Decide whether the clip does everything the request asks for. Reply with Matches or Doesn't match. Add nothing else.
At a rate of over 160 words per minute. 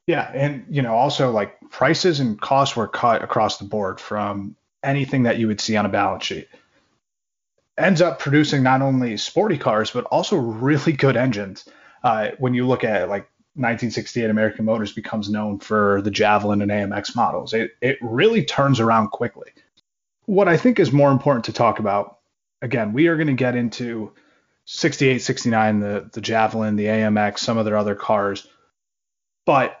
Matches